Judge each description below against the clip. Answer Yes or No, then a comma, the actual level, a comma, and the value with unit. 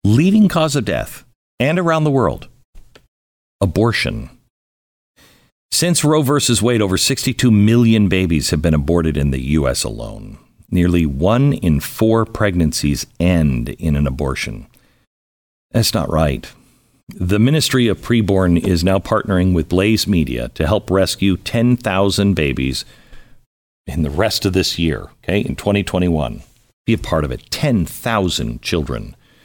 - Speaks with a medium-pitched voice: No, very low, 95 Hz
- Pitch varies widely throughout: Yes, wide, 6.6 semitones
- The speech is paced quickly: No, slow, 135 wpm